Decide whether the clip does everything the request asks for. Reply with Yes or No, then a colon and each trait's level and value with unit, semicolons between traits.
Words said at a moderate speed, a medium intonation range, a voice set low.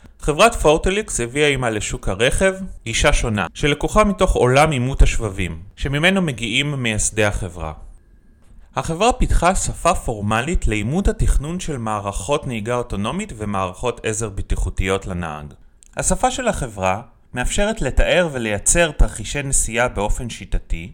No: average, 120 wpm; wide, 6.8 semitones; low, 120 Hz